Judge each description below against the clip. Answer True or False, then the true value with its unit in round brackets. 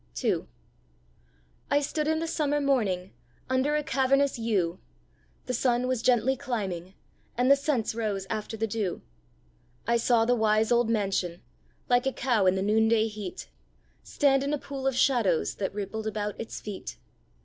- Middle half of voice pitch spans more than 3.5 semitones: True (4.3 semitones)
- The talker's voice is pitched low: False (230 Hz)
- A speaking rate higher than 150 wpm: True (160 wpm)